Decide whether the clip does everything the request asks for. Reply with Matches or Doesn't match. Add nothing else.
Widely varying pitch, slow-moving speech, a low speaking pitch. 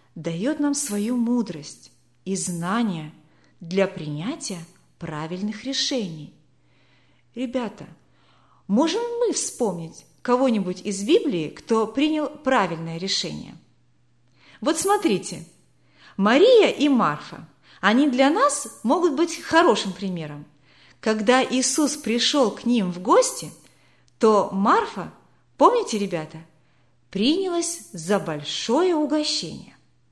Doesn't match